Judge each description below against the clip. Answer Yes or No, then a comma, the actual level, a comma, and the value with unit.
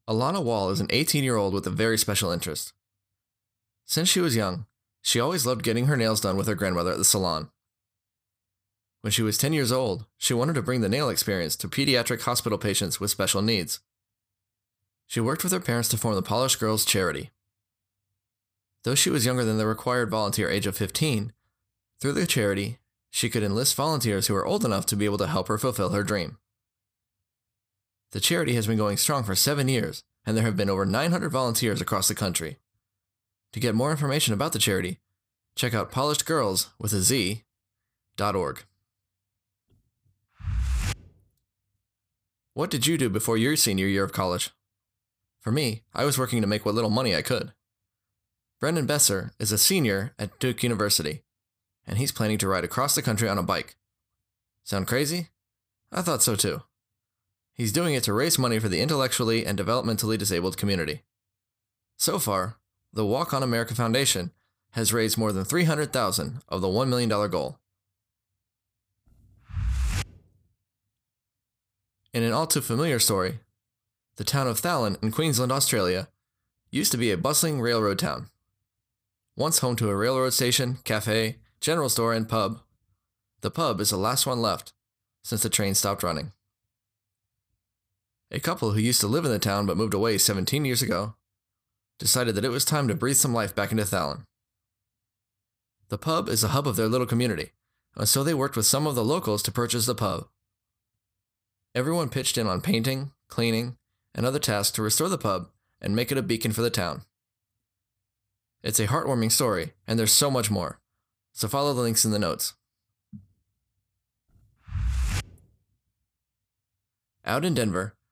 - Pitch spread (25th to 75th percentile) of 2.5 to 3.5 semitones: Yes, average, 2.9 semitones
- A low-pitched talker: Yes, low, 110 Hz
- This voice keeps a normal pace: Yes, average, 170 wpm